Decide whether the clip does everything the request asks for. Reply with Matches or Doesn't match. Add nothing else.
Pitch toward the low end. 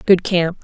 Doesn't match